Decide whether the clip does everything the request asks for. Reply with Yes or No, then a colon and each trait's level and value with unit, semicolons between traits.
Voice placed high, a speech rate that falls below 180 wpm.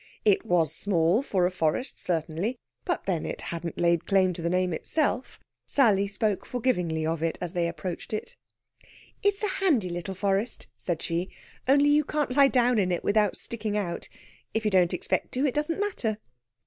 No: high, 195 Hz; average, 185 wpm